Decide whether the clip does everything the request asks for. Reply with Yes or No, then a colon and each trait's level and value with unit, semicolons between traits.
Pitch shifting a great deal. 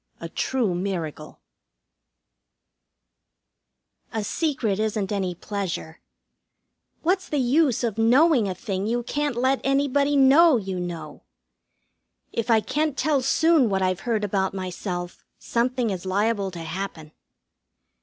Yes: wide, 6.0 semitones